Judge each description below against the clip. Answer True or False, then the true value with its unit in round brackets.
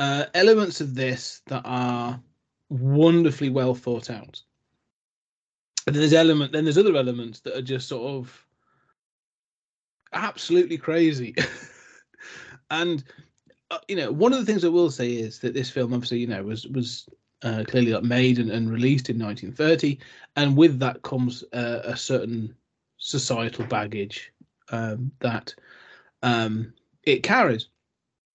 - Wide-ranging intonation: False (3.6 semitones)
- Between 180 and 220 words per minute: False (140 wpm)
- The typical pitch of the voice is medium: False (130 Hz)